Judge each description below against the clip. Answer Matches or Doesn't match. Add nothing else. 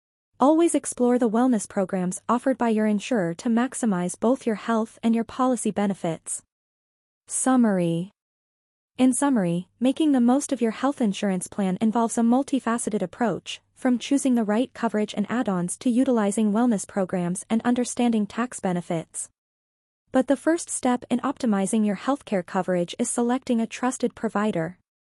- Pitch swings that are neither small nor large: Matches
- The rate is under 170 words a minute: Matches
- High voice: Matches